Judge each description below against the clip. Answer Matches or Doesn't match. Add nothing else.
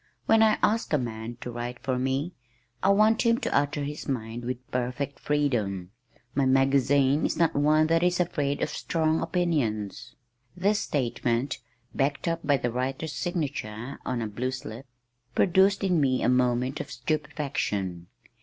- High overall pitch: Doesn't match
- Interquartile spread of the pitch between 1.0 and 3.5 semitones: Doesn't match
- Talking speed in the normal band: Matches